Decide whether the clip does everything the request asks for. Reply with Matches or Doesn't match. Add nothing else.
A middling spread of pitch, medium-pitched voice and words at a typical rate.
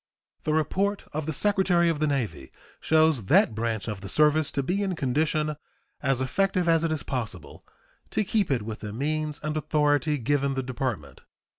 Matches